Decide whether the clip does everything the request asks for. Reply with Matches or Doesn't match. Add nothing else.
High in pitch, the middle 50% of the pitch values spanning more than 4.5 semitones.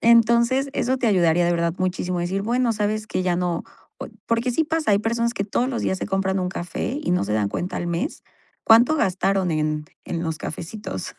Matches